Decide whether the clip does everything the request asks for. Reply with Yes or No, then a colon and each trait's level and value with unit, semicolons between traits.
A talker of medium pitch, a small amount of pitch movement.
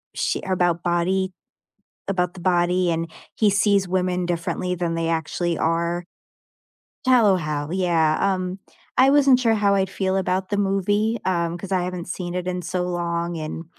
Yes: medium, 180 Hz; narrow, 1.9 semitones